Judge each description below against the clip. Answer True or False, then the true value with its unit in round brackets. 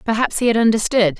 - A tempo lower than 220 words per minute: True (200 wpm)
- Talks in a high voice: True (220 Hz)